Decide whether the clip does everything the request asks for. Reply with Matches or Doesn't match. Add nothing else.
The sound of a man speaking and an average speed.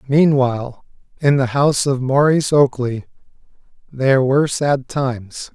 Doesn't match